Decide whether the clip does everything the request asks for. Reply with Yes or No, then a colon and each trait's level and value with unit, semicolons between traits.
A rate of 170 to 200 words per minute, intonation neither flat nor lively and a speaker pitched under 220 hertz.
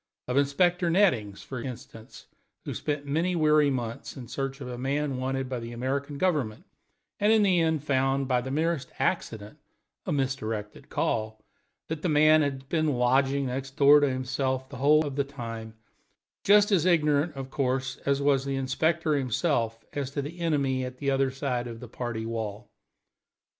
Yes: average, 180 wpm; average, 3.0 semitones; low, 135 Hz